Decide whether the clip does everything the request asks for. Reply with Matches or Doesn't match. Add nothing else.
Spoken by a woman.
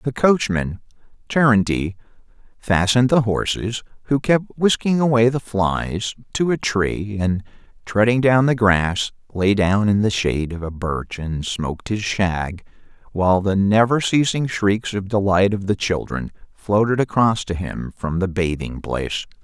Doesn't match